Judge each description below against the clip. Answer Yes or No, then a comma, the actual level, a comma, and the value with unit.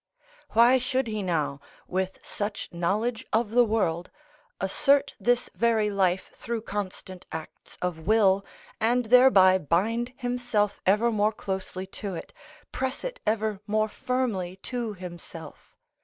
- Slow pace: Yes, slow, 130 wpm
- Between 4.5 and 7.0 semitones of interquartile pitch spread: No, average, 4.1 semitones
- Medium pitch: No, high, 210 Hz